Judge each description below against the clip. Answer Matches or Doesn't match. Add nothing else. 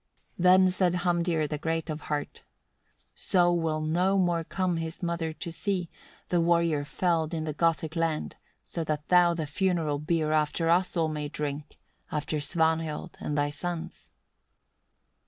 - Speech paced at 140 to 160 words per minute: Matches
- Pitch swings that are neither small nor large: Doesn't match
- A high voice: Doesn't match